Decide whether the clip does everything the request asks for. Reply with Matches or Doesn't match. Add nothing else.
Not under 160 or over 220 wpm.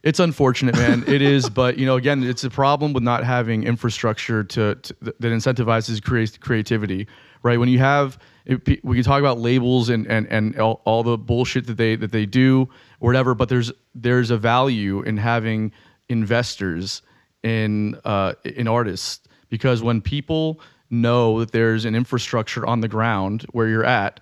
Matches